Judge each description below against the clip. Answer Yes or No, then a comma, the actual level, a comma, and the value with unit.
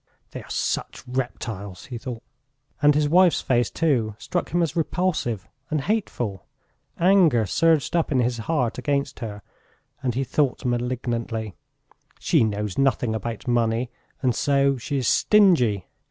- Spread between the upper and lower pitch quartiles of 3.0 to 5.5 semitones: Yes, average, 4.7 semitones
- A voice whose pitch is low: Yes, low, 125 Hz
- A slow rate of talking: No, average, 145 wpm